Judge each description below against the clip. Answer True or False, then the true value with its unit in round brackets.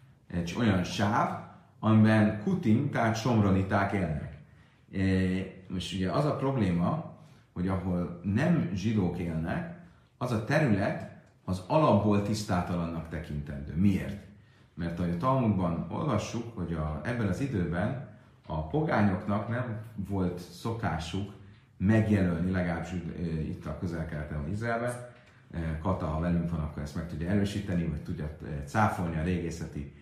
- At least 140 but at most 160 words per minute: False (125 wpm)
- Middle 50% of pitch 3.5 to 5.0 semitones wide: True (4.2 semitones)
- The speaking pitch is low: True (95 Hz)